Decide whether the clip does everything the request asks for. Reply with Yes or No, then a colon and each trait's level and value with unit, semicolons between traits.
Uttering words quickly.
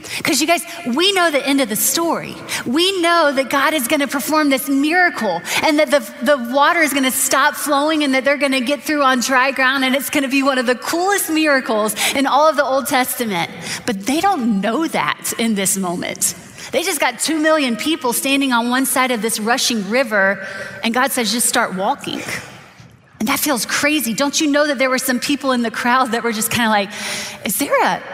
Yes: fast, 230 wpm